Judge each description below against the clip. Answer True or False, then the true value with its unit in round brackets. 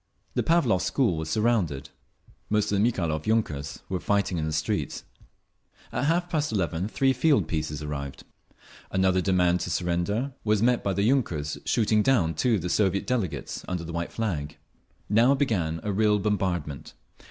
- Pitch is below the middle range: True (95 Hz)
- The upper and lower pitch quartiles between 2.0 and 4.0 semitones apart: False (5.4 semitones)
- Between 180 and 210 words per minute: False (165 wpm)